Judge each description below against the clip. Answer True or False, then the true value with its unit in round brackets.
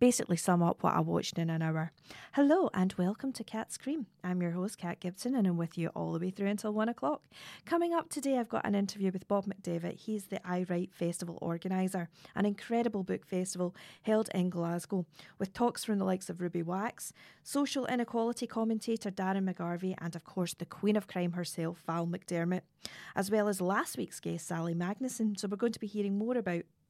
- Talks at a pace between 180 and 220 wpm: True (205 wpm)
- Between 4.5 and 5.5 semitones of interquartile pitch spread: False (3.9 semitones)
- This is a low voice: False (190 Hz)